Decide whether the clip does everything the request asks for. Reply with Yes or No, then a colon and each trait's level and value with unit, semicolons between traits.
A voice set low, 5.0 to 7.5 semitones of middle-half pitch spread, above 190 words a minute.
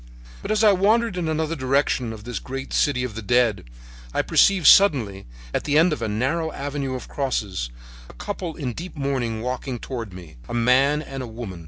Yes: low, 130 Hz; wide, 5.4 semitones; average, 200 wpm